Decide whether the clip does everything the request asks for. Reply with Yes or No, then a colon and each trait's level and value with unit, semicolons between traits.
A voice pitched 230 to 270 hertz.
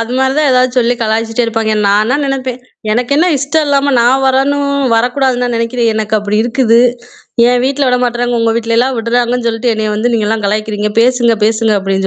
Yes: high, 240 Hz